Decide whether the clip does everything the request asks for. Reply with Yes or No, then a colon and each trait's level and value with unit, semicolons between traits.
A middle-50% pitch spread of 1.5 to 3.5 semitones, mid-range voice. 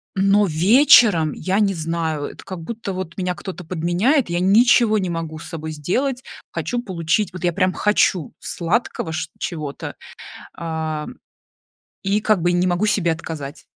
No: average, 4.1 semitones; medium, 180 Hz